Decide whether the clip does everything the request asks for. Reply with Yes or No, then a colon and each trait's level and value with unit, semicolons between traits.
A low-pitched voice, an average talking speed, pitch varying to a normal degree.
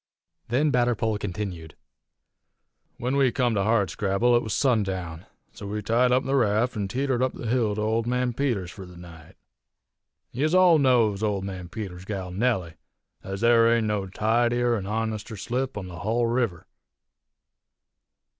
Yes: low, 110 Hz; average, 160 wpm; average, 3.9 semitones